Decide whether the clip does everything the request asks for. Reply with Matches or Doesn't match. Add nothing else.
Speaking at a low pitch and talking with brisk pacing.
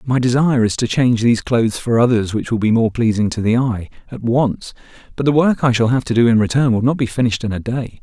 Matches